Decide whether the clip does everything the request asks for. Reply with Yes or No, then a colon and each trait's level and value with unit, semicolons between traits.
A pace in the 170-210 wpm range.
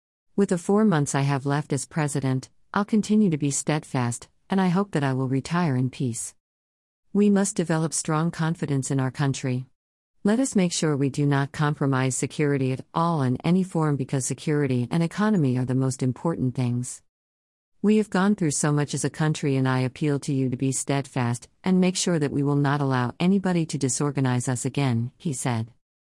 Yes: average, 200 wpm